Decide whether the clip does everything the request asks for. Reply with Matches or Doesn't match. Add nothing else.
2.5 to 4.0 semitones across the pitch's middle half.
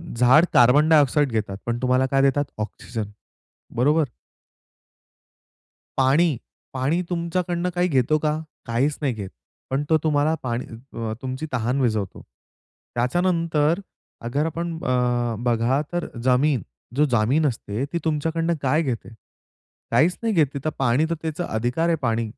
Doesn't match